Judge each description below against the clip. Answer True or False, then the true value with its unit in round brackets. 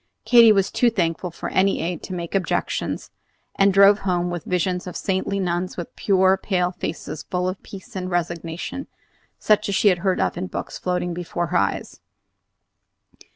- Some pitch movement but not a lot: False (1.9 semitones)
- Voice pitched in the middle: True (180 Hz)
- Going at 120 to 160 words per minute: False (175 wpm)